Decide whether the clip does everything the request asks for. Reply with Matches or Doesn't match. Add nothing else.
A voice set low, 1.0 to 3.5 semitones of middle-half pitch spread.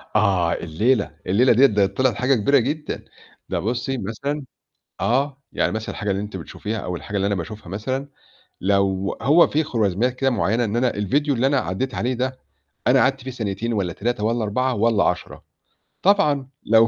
Doesn't match